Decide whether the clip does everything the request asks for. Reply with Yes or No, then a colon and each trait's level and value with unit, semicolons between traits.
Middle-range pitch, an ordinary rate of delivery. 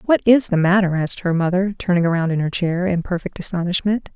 No: medium, 180 Hz; fast, 215 wpm